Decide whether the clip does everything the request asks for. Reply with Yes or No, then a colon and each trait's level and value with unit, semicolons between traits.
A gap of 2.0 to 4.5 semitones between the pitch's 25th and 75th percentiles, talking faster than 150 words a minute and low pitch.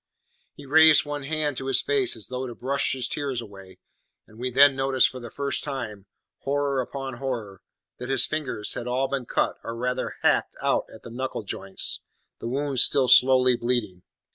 Yes: average, 2.8 semitones; average, 190 wpm; low, 130 Hz